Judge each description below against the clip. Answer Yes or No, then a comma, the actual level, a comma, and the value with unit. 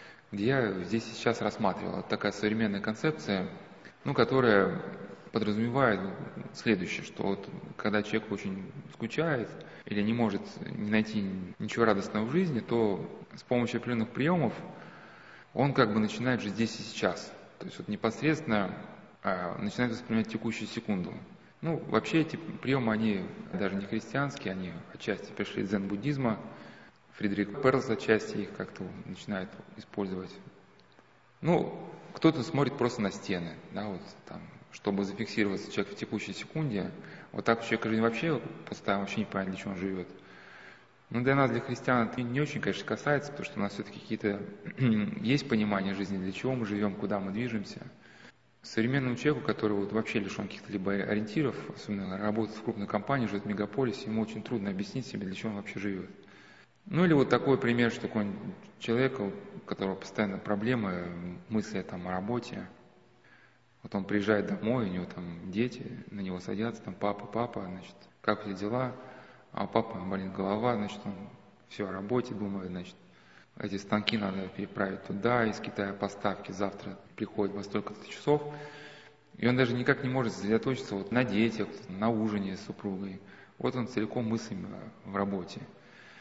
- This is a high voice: No, low, 110 Hz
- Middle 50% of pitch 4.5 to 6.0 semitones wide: No, average, 3.5 semitones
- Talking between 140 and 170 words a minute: Yes, fast, 160 wpm